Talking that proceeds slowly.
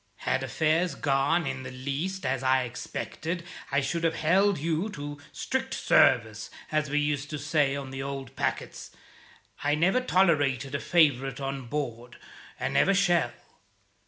No: average, 155 wpm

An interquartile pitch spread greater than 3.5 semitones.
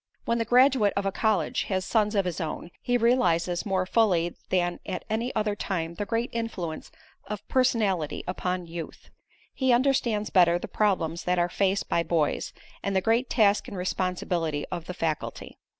Yes: average, 4.4 semitones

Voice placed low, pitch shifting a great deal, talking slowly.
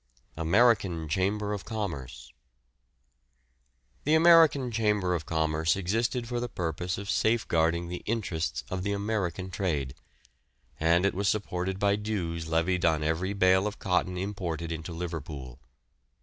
No: very low, 90 Hz; average, 4.0 semitones; slow, 130 wpm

